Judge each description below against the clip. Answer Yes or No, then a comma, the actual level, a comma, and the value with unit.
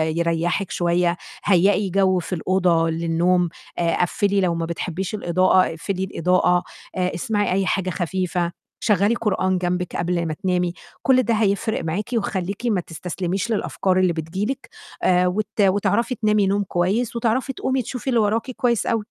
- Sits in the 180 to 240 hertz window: Yes, medium, 185 Hz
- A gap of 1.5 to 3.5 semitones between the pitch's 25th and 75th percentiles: Yes, average, 3.0 semitones